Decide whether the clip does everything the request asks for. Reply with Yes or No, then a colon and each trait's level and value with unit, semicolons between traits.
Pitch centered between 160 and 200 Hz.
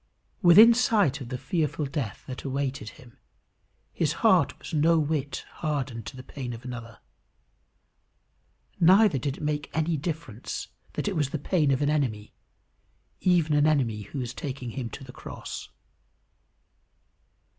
No: medium, 140 Hz